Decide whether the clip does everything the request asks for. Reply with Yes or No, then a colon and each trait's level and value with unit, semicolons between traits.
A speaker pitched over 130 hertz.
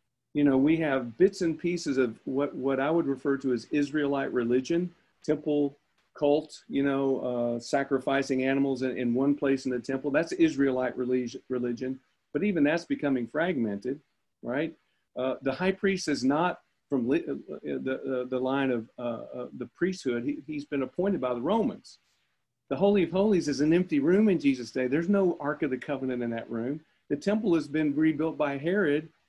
Yes: medium, 140 Hz